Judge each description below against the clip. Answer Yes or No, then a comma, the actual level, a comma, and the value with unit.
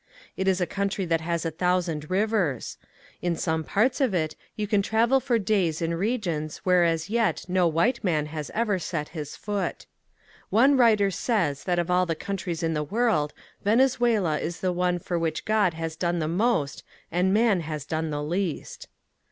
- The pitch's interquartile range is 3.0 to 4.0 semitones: No, average, 4.4 semitones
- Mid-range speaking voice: Yes, medium, 180 Hz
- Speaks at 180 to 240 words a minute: Yes, average, 185 wpm